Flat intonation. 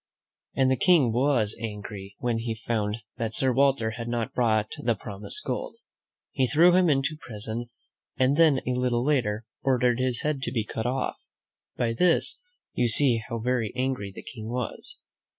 No: average, 3.1 semitones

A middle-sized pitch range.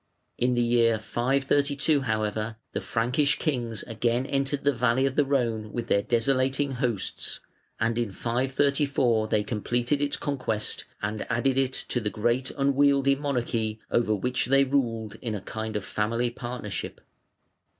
Yes: average, 3.5 semitones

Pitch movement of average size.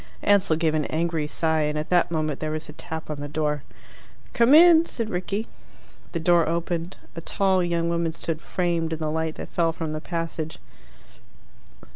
No: narrow, 1.9 semitones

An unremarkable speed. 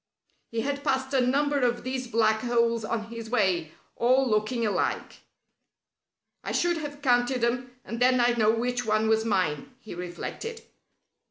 Yes: average, 160 wpm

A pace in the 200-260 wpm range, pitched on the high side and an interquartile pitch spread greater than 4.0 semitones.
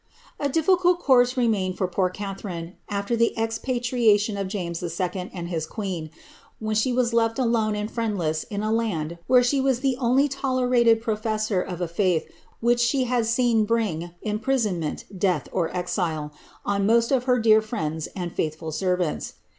No: average, 160 wpm; high, 215 Hz; average, 4.9 semitones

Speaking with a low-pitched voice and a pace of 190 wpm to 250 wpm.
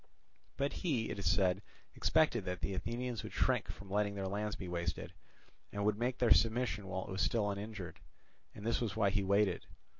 Yes: low, 100 Hz; average, 200 wpm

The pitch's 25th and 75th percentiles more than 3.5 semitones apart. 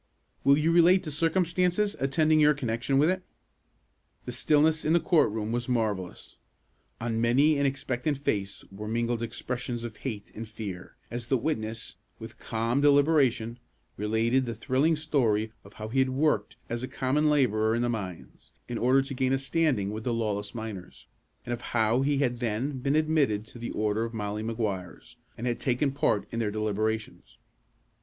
Yes: average, 4.4 semitones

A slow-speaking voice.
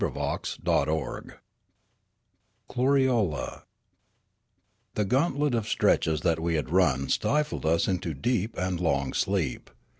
Yes: slow, 110 wpm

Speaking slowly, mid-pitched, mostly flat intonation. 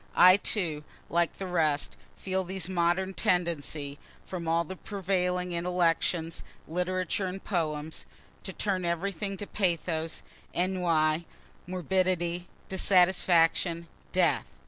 Yes: slow, 105 wpm; medium, 180 Hz; narrow, 2.1 semitones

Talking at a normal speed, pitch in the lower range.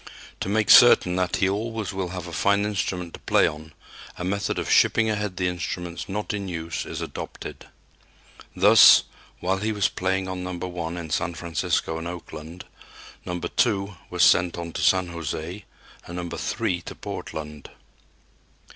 Yes: average, 165 wpm; very low, 90 Hz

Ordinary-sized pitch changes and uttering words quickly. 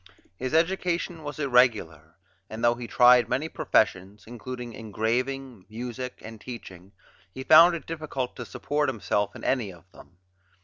No: average, 4.0 semitones; average, 145 wpm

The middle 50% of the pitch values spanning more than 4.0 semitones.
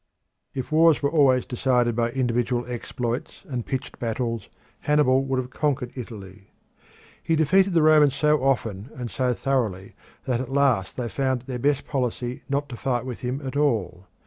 No: average, 2.8 semitones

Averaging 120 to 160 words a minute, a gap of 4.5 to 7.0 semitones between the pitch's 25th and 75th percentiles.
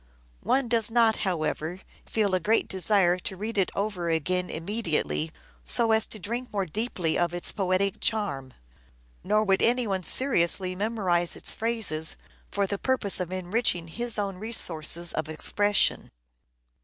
No: average, 150 wpm; average, 4.1 semitones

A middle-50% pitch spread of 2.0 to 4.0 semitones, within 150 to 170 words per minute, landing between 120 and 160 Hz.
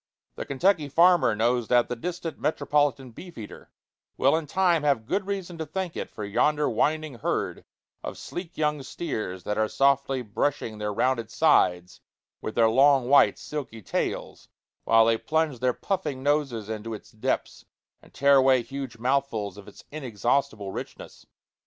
No: average, 5.1 semitones; average, 160 wpm; low, 135 Hz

